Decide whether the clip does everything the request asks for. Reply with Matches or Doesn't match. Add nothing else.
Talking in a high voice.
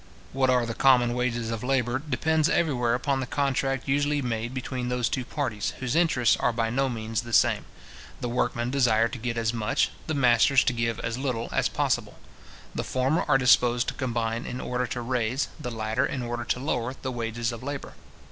Doesn't match